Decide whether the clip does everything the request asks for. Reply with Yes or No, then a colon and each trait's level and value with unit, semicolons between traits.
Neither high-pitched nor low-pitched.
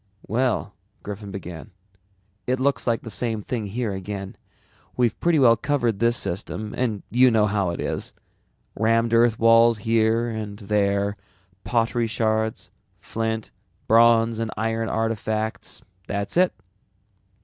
No: low, 115 Hz